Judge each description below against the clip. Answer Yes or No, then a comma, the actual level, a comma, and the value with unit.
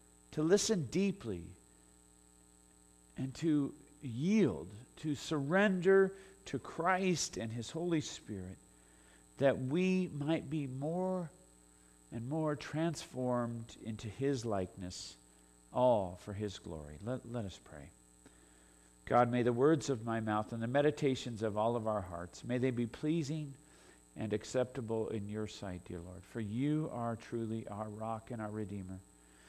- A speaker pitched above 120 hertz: No, low, 115 Hz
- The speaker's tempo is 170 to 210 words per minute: No, average, 140 wpm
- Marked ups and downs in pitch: Yes, wide, 8.5 semitones